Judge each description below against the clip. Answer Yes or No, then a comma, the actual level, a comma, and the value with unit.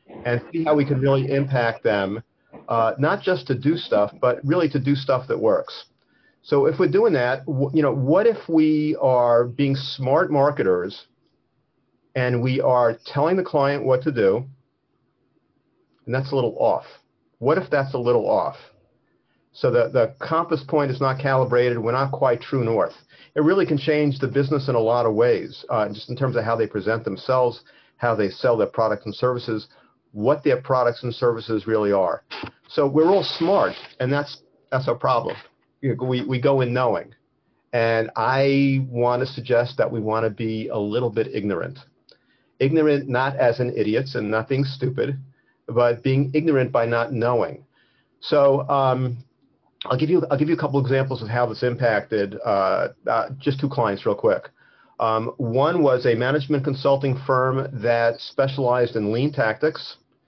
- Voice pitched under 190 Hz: Yes, low, 135 Hz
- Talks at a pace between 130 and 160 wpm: No, average, 180 wpm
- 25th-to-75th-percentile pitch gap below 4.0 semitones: Yes, average, 3.3 semitones